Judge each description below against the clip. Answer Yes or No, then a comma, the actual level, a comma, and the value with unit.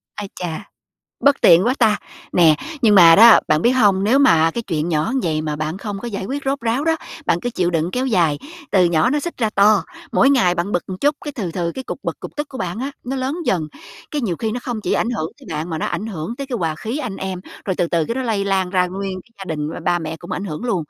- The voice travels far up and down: Yes, wide, 6.2 semitones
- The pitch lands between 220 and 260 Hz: No, high, 195 Hz